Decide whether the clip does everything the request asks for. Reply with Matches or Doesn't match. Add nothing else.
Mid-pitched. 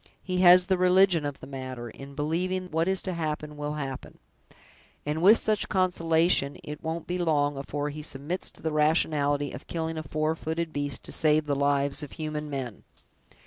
Matches